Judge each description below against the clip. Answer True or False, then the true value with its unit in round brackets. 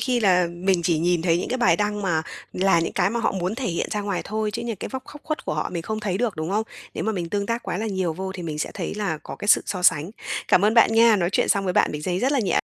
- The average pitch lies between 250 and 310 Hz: False (195 Hz)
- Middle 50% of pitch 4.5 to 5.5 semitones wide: False (3.9 semitones)